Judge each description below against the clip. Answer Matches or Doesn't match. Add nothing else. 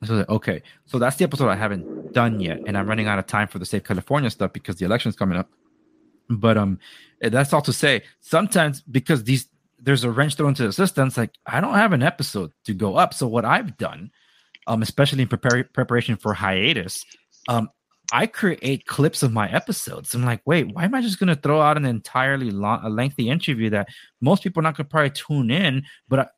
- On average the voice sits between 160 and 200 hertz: Doesn't match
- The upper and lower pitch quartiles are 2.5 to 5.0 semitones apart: Doesn't match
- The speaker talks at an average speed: Doesn't match